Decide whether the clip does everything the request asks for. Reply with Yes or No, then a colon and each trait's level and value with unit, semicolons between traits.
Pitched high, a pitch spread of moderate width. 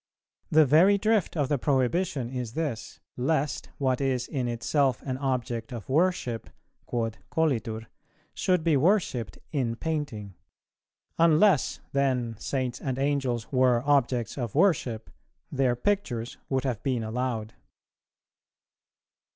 No: low, 130 Hz; average, 4.1 semitones